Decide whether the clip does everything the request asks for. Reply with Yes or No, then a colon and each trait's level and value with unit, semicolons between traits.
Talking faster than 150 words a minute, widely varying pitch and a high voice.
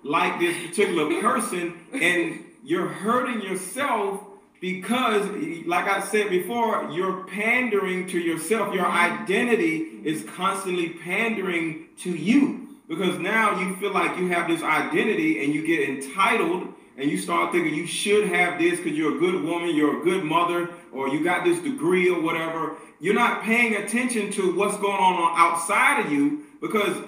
Yes: average, 160 wpm; wide, 5.7 semitones; high, 195 Hz